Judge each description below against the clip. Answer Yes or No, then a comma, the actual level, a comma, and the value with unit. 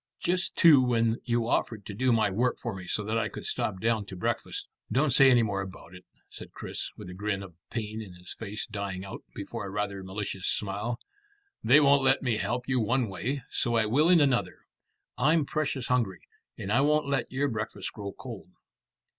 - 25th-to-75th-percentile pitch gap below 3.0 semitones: No, average, 4.5 semitones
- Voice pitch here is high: No, low, 115 Hz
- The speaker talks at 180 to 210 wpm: Yes, fast, 205 wpm